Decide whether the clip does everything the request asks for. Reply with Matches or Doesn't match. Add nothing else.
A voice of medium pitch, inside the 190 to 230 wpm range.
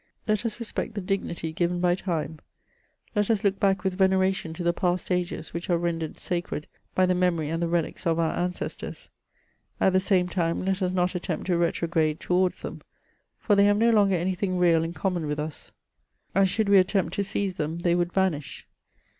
Matches